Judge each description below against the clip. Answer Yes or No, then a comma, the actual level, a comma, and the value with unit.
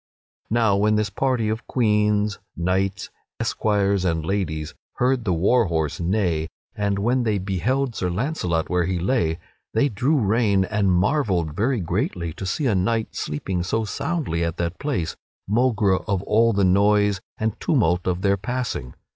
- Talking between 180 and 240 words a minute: No, average, 155 wpm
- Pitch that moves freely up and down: No, average, 4.0 semitones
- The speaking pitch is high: No, low, 100 Hz